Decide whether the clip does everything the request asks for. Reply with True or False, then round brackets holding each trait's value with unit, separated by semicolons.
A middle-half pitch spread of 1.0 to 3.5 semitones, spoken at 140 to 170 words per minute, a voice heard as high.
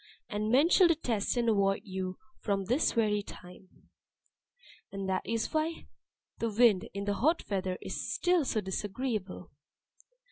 False (4.1 semitones; 145 wpm; 210 Hz)